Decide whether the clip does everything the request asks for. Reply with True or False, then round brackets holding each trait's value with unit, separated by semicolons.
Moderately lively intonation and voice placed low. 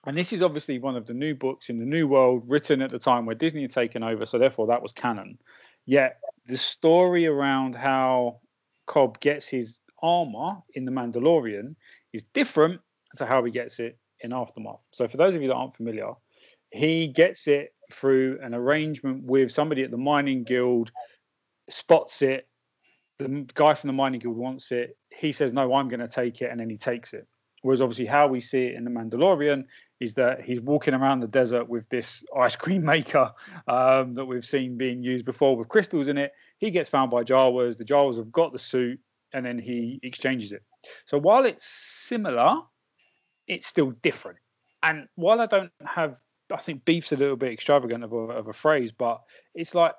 True (3.3 semitones; 130 Hz)